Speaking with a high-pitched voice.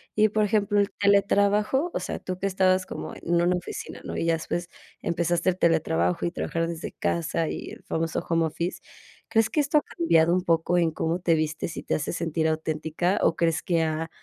No: medium, 170 Hz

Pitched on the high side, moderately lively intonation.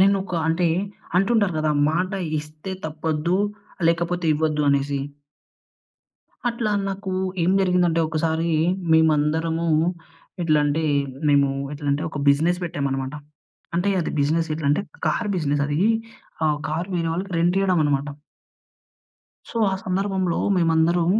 No: medium, 165 Hz; average, 3.1 semitones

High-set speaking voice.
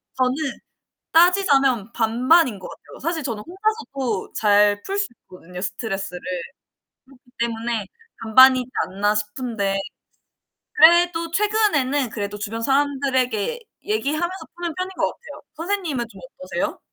Yes: very high, 255 Hz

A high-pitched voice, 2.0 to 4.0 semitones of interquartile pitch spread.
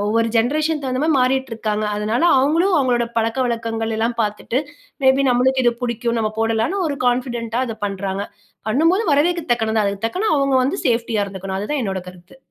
Yes: high, 235 Hz; average, 3.4 semitones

